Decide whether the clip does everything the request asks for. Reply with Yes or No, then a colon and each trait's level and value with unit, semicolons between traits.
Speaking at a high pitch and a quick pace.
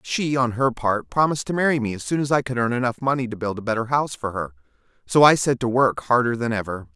No: low, 120 Hz; fast, 270 wpm